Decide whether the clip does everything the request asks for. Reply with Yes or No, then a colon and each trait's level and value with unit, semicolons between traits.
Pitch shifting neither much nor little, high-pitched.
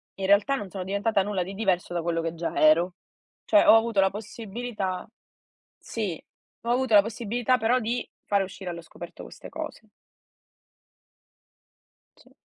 Yes: average, 3.8 semitones; high, 200 Hz